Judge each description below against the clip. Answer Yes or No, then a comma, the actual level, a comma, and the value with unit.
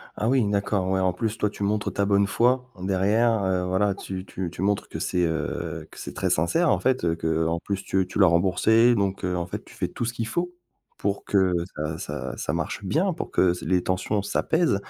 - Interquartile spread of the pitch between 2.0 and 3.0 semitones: No, average, 3.5 semitones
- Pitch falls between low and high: No, low, 100 Hz